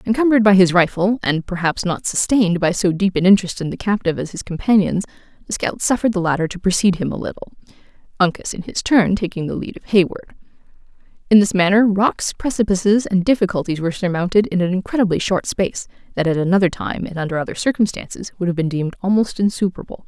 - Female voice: Yes, female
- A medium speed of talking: Yes, average, 195 wpm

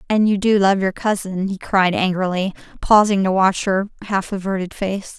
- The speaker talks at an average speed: Yes, average, 185 wpm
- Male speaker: No, female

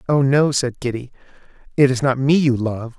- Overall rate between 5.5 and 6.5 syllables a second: No, 5.1 syllables/s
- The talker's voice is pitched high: No, low, 130 Hz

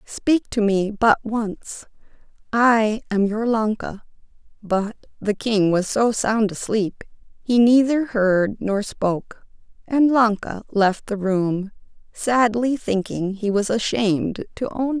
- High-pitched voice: Yes, high, 215 Hz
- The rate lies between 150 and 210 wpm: No, slow, 135 wpm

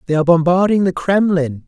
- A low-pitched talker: No, medium, 170 Hz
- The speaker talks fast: No, average, 180 wpm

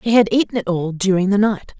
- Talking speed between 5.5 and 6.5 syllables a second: Yes, 5.9 syllables/s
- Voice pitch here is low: No, high, 200 Hz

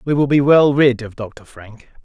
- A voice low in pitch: Yes, low, 130 Hz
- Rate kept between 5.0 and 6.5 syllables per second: No, 4.4 syllables/s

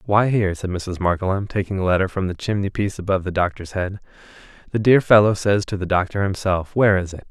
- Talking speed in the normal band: No, fast, 215 wpm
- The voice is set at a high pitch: No, very low, 95 Hz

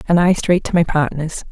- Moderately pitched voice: Yes, medium, 165 Hz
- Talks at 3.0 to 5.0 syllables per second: No, 5.3 syllables/s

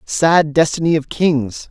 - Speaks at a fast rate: No, average, 140 wpm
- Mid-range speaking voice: Yes, medium, 155 Hz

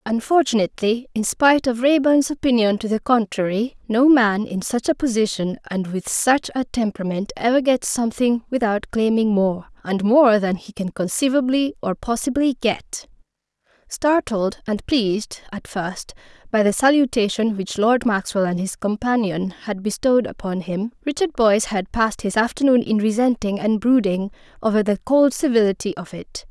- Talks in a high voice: Yes, high, 225 Hz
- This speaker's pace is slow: No, average, 155 wpm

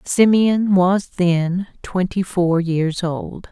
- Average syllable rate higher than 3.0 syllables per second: No, 2.8 syllables/s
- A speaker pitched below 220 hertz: Yes, medium, 185 Hz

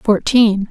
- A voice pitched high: Yes, high, 215 Hz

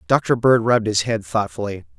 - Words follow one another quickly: No, average, 180 wpm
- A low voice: Yes, low, 110 Hz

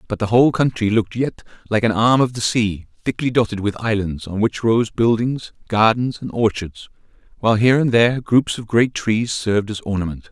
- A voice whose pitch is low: Yes, low, 110 Hz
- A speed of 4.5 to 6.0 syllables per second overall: Yes, 5.4 syllables/s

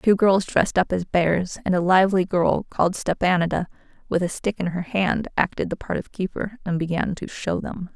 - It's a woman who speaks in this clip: Yes, female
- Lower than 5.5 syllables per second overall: Yes, 5.3 syllables/s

